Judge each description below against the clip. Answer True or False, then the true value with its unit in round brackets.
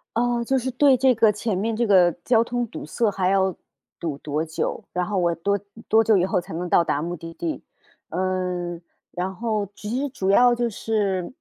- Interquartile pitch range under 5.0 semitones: True (4.4 semitones)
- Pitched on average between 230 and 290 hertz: False (195 Hz)